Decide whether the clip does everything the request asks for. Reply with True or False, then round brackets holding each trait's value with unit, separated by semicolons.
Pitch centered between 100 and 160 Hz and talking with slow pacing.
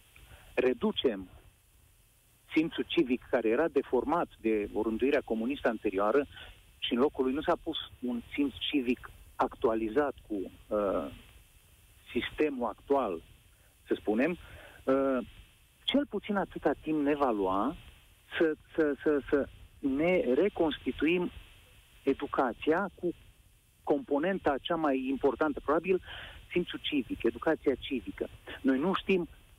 True (135 Hz; 110 wpm)